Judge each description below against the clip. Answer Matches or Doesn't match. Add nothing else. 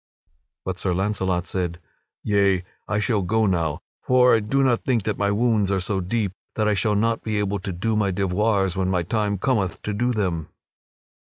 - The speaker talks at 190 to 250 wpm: Matches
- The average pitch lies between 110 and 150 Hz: Doesn't match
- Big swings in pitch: Doesn't match